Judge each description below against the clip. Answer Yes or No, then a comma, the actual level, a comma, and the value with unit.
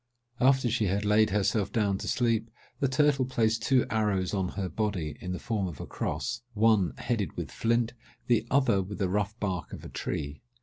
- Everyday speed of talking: Yes, average, 190 wpm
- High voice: No, low, 105 Hz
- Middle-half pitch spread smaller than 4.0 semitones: Yes, average, 3.5 semitones